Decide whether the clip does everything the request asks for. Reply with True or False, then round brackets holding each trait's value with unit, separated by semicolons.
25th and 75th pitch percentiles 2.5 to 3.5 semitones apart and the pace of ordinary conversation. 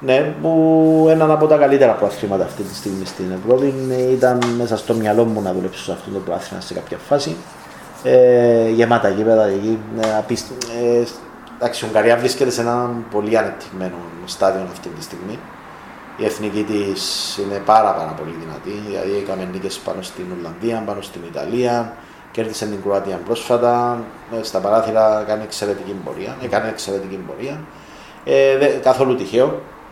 True (3.2 semitones; 150 wpm)